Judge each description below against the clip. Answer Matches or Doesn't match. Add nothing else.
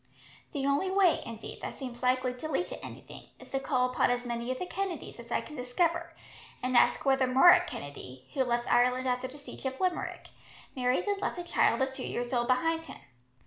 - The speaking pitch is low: Doesn't match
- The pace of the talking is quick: Matches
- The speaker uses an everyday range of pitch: Matches